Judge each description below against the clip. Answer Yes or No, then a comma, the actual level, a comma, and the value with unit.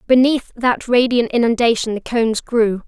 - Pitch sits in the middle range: No, high, 235 Hz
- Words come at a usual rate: Yes, average, 145 wpm